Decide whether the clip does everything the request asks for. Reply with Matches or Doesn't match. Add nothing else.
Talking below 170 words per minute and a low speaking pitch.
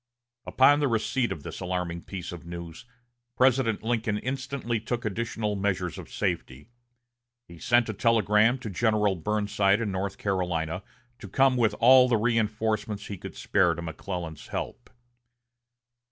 Matches